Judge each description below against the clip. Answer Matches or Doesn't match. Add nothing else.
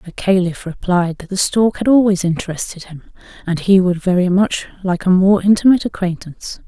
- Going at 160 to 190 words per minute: Matches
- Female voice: Matches